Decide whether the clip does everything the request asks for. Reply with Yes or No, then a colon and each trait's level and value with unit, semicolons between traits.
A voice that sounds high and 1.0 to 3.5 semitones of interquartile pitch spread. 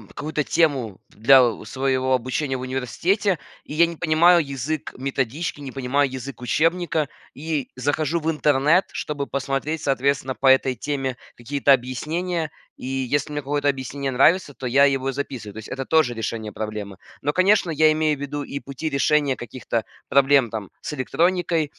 No: medium, 140 Hz; average, 3.1 semitones